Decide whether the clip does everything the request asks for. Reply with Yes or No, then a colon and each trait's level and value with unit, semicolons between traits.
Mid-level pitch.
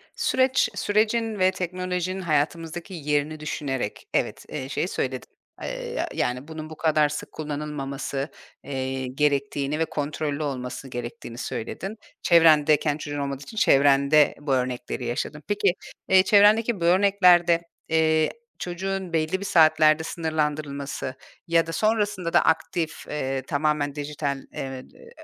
Yes: medium, 155 Hz